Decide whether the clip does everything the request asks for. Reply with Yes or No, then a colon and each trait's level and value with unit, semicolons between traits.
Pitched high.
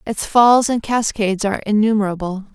Yes: high, 210 Hz